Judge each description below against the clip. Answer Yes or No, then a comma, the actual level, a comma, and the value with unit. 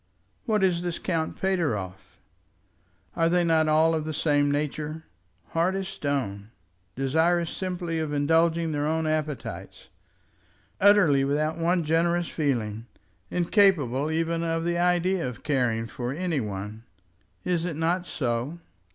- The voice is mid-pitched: Yes, medium, 160 Hz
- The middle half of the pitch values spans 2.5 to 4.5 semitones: Yes, average, 3.3 semitones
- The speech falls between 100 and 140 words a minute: Yes, slow, 135 wpm